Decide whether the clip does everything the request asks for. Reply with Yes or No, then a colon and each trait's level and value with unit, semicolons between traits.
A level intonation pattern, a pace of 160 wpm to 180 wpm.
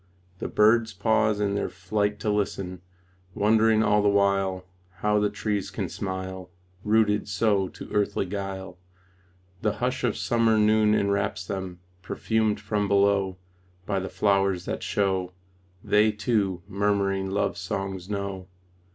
No: narrow, 1.7 semitones; slow, 135 wpm